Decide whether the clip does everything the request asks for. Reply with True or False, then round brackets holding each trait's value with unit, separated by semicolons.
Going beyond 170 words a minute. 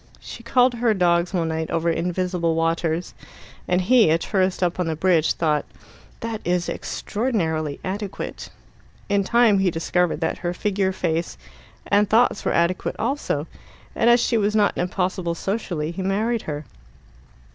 False (155 wpm)